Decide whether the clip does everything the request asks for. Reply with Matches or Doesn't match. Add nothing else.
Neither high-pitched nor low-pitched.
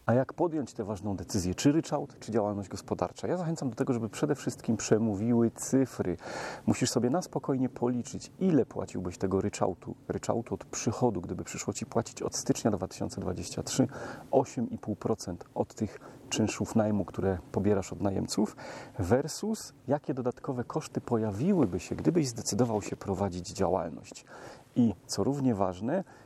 Doesn't match